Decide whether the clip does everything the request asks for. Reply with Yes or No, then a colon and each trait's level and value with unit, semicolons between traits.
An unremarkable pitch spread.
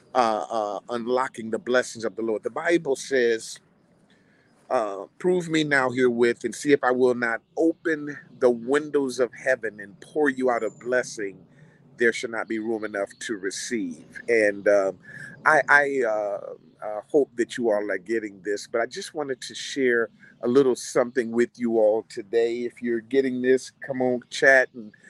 Yes: average, 4.0 semitones